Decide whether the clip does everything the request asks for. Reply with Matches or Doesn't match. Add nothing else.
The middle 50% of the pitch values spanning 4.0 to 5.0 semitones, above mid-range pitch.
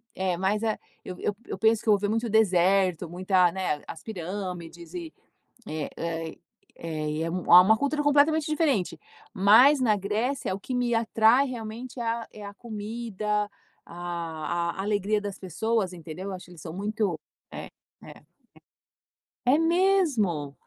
Matches